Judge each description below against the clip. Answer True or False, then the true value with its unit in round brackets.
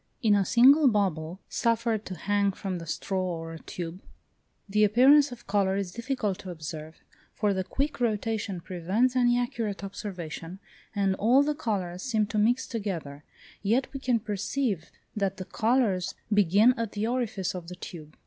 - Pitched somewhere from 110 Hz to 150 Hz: False (205 Hz)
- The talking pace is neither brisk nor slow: True (165 wpm)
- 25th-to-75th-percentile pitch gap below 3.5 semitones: False (4.3 semitones)